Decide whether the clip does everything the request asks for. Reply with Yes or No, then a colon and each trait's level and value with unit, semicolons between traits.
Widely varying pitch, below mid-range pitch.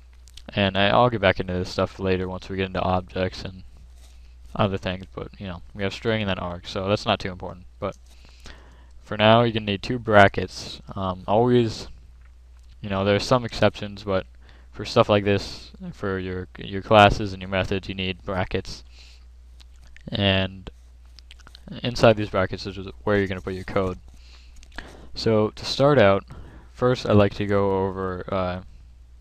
Yes: wide, 8.0 semitones; very low, 95 Hz